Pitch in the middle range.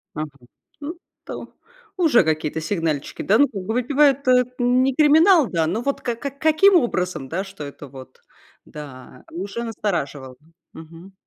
No: high, 200 Hz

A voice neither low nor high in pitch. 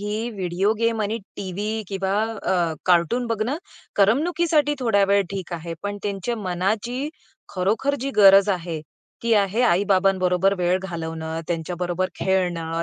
No: high, 195 Hz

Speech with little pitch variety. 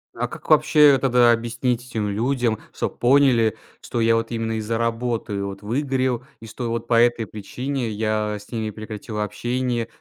Yes: narrow, 2.2 semitones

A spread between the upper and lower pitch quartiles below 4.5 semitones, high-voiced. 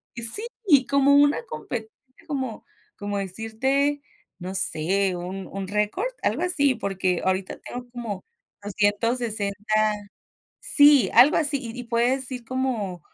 No: wide, 5.4 semitones; high, 230 Hz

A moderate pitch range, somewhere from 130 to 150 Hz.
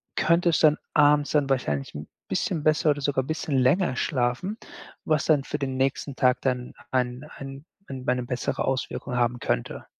Yes: average, 3.0 semitones; low, 135 Hz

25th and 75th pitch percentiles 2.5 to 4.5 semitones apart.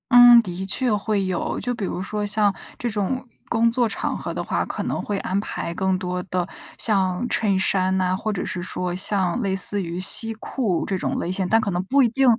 Yes: average, 3.3 semitones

